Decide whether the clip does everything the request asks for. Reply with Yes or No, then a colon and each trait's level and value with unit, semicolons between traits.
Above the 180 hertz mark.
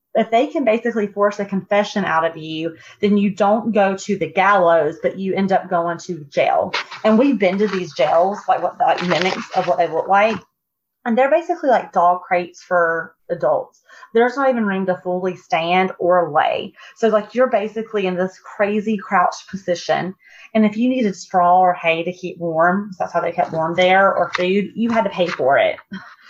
Yes: high, 190 Hz